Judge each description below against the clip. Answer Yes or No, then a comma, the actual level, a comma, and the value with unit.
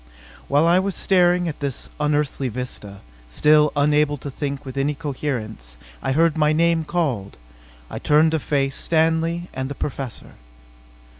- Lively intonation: No, average, 3.1 semitones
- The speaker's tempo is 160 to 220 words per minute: No, average, 150 wpm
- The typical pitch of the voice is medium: Yes, medium, 150 Hz